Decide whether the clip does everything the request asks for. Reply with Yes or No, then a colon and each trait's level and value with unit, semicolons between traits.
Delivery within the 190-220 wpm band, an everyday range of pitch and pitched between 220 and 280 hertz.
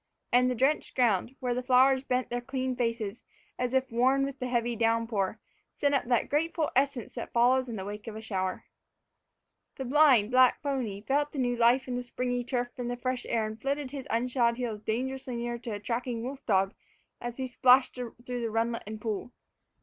No: average, 200 wpm; narrow, 2.1 semitones; high, 245 Hz